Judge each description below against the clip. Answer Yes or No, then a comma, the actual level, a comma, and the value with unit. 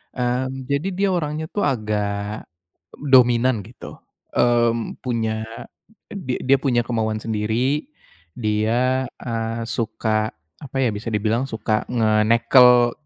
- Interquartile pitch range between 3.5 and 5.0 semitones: No, average, 2.9 semitones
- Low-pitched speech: Yes, low, 120 Hz